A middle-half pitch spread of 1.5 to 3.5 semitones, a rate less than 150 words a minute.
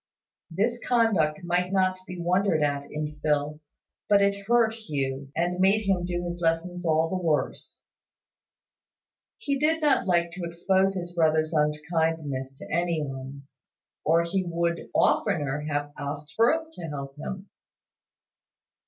No: average, 4.0 semitones; average, 140 wpm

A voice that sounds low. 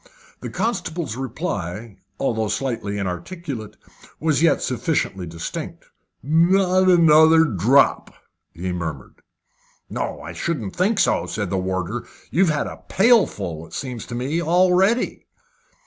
Yes: low, 130 Hz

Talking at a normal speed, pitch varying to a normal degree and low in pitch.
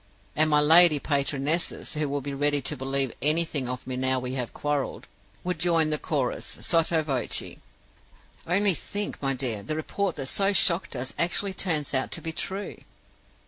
No: average, 175 wpm; average, 3.8 semitones; medium, 150 Hz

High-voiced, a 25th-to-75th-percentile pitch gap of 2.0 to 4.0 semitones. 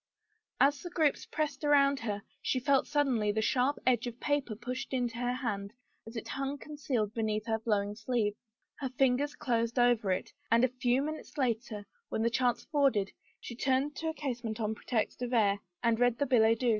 Yes: high, 245 Hz; average, 3.5 semitones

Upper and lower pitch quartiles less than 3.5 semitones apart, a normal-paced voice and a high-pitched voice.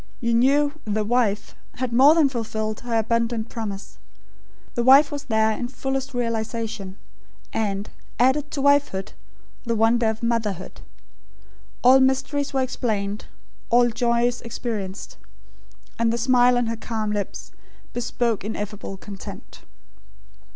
No: average, 2.8 semitones; slow, 125 wpm; high, 235 Hz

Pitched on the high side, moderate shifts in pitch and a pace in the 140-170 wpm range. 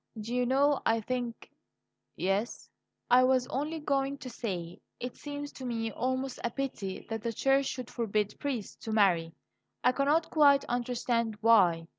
Yes: high, 245 Hz; average, 3.6 semitones; average, 165 wpm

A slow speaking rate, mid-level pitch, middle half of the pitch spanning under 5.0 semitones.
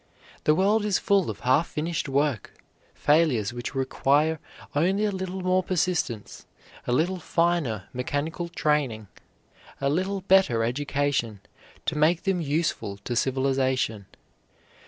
No: slow, 125 wpm; medium, 150 Hz; wide, 5.4 semitones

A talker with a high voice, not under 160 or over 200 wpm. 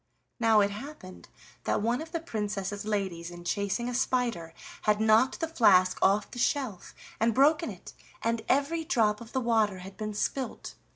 Yes: high, 220 Hz; average, 175 wpm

